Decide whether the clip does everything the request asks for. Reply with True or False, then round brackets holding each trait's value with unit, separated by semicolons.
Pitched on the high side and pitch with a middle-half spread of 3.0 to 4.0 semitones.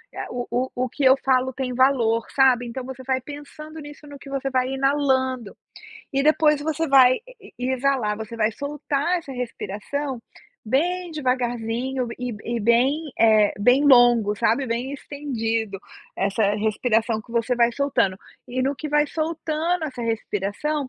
True (260 Hz; 3.6 semitones)